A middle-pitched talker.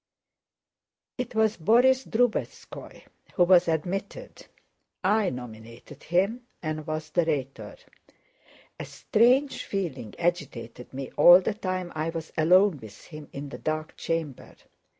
Yes: medium, 170 Hz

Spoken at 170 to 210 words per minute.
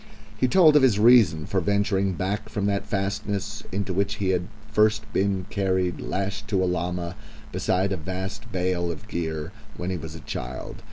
Yes: average, 180 wpm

